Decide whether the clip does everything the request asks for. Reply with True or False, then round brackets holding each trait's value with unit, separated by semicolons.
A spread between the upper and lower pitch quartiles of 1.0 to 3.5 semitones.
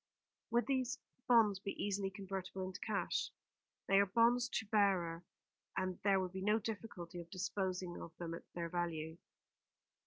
True (3.0 semitones)